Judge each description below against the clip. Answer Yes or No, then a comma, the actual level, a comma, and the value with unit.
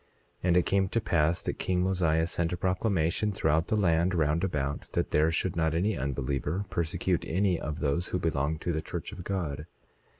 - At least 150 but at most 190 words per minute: No, average, 200 wpm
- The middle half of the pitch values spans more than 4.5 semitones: No, average, 2.8 semitones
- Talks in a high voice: No, very low, 85 Hz